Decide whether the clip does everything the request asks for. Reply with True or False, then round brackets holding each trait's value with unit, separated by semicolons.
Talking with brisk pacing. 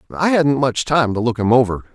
True (245 wpm)